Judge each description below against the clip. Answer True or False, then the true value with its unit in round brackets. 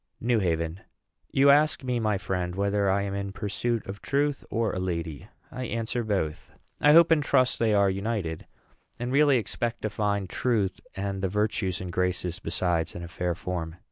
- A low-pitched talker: True (100 Hz)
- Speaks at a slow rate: False (185 wpm)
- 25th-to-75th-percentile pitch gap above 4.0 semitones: True (4.5 semitones)